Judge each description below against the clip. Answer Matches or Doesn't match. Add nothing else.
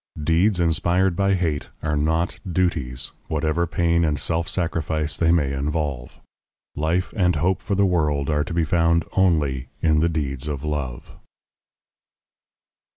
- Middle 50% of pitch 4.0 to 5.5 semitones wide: Doesn't match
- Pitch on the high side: Doesn't match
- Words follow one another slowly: Doesn't match